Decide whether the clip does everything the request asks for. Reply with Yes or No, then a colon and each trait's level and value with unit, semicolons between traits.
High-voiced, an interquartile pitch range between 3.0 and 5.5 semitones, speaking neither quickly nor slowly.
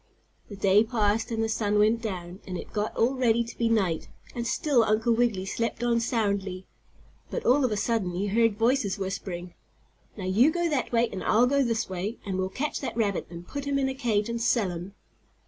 No: high, 225 Hz; average, 3.5 semitones; fast, 215 wpm